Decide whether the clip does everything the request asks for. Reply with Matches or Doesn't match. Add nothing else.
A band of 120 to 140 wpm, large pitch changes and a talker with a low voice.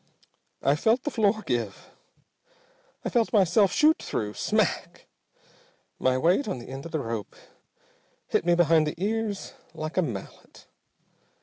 Doesn't match